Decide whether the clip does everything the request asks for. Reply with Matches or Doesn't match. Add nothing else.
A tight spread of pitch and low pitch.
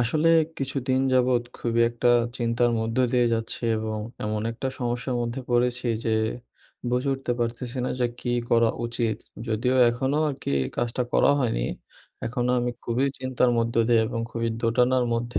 Matches